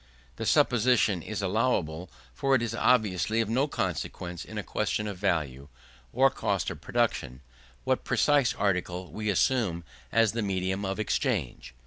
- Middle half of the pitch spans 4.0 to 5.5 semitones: Yes, average, 4.3 semitones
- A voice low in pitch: Yes, low, 100 Hz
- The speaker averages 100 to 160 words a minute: Yes, average, 150 wpm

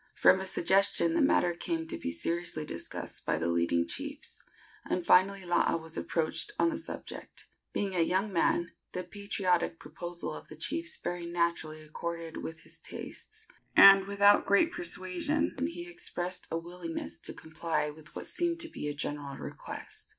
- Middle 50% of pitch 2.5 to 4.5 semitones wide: Yes, average, 3.8 semitones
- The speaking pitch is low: No, medium, 175 Hz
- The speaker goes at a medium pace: Yes, average, 165 wpm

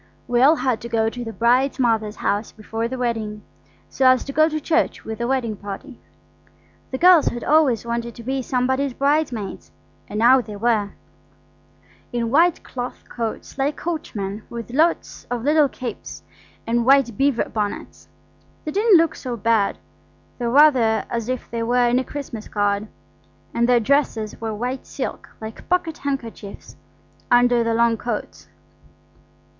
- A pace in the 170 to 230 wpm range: No, average, 160 wpm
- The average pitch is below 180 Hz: No, high, 240 Hz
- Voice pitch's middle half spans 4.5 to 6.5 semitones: No, average, 3.3 semitones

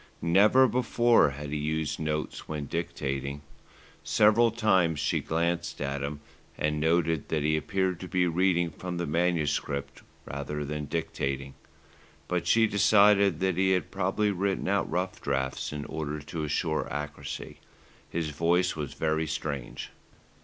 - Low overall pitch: Yes, very low, 80 Hz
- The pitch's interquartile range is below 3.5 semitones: No, average, 4.0 semitones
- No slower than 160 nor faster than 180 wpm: No, average, 145 wpm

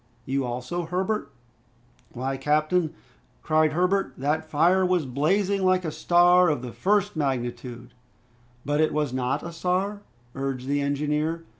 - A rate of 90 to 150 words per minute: Yes, average, 140 wpm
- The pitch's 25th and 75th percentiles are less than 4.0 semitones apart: No, average, 4.9 semitones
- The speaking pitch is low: No, medium, 155 Hz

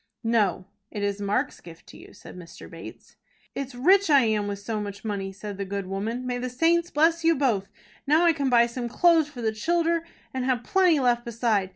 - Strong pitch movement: Yes, wide, 6.4 semitones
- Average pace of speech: No, fast, 215 wpm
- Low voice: No, high, 240 Hz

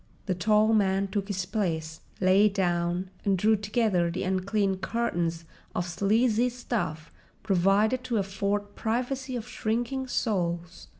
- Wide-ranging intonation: No, average, 3.4 semitones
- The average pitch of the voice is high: Yes, high, 200 Hz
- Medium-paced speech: No, slow, 130 wpm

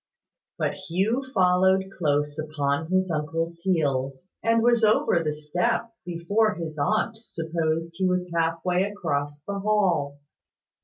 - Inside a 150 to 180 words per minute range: No, slow, 135 wpm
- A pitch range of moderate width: Yes, average, 3.9 semitones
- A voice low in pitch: No, medium, 170 Hz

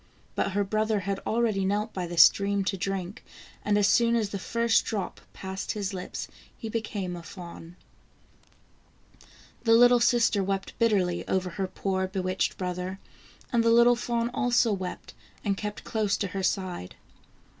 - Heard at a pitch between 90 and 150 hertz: No, high, 200 Hz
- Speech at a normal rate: Yes, average, 160 wpm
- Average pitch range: Yes, average, 3.1 semitones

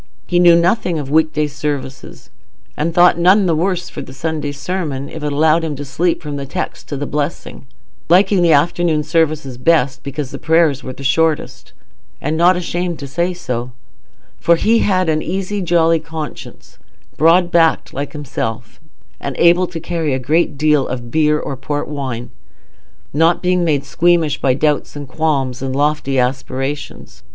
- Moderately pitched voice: Yes, medium, 155 Hz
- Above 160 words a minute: Yes, average, 170 wpm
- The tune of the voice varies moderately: Yes, average, 3.4 semitones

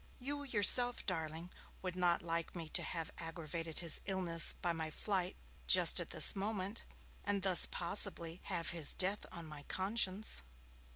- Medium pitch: Yes, medium, 180 Hz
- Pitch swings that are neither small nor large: Yes, average, 3.1 semitones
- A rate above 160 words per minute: No, average, 155 wpm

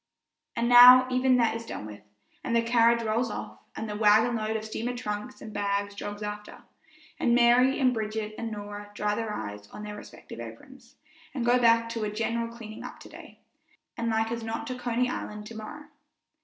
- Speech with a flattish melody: Yes, narrow, 2.3 semitones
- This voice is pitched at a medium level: No, high, 225 Hz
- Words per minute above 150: Yes, average, 195 wpm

